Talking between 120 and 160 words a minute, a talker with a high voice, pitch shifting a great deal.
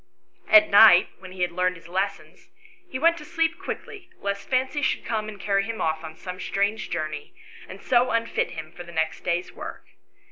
No: average, 200 wpm; high, 200 Hz; wide, 6.1 semitones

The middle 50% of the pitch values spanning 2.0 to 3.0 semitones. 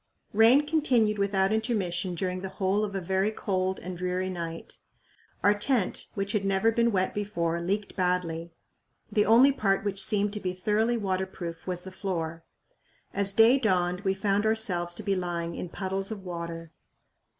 Yes: average, 2.7 semitones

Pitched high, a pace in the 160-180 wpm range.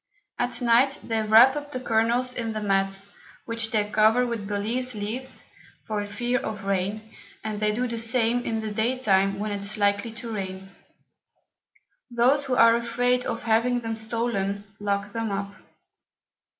Yes: high, 225 Hz; average, 165 wpm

